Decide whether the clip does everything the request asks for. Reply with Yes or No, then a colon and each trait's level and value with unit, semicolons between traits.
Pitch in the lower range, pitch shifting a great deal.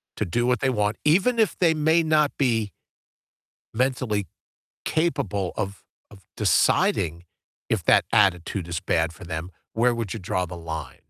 Yes: low, 105 Hz; wide, 7.4 semitones